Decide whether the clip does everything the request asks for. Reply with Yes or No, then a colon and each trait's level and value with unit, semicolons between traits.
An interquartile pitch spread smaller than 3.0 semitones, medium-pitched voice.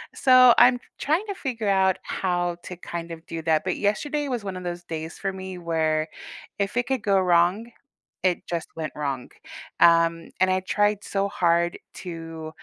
No: average, 3.7 semitones; medium, 180 Hz